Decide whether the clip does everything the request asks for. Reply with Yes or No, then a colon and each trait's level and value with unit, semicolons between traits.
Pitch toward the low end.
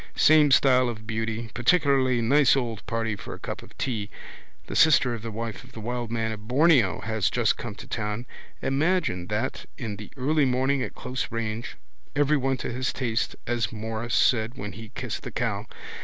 Yes: low, 120 Hz